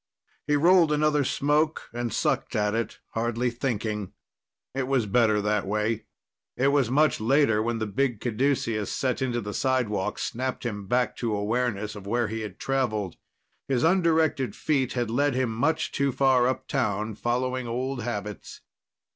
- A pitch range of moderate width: Yes, average, 4.0 semitones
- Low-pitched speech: Yes, low, 120 Hz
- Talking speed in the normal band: Yes, average, 155 wpm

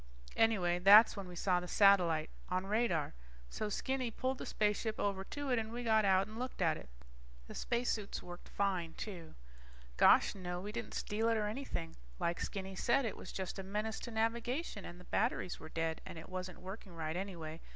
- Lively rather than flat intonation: No, average, 4.0 semitones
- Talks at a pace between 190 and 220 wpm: Yes, average, 200 wpm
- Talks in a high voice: Yes, high, 200 Hz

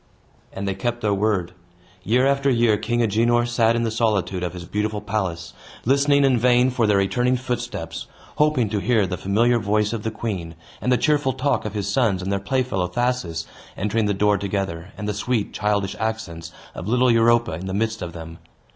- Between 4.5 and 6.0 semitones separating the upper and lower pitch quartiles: No, average, 3.8 semitones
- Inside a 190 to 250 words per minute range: Yes, average, 200 wpm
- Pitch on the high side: No, low, 110 Hz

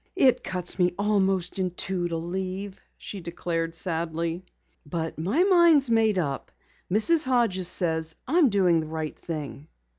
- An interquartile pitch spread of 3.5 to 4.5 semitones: Yes, average, 4.2 semitones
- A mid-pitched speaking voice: Yes, medium, 180 Hz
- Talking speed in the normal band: Yes, average, 150 wpm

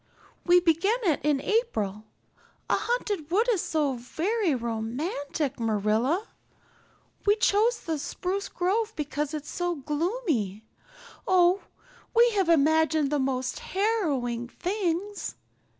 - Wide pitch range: Yes, wide, 6.7 semitones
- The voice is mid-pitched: No, very high, 320 Hz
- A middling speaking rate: No, slow, 115 wpm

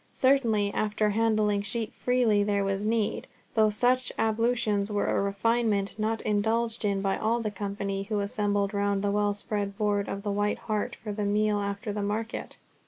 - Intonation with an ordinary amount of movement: No, narrow, 1.7 semitones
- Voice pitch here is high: Yes, high, 210 Hz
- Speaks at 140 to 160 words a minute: No, average, 175 wpm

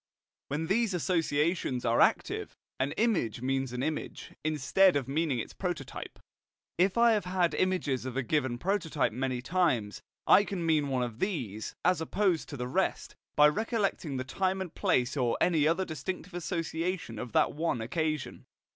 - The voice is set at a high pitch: No, medium, 155 Hz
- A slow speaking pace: No, average, 165 wpm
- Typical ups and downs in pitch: No, wide, 5.8 semitones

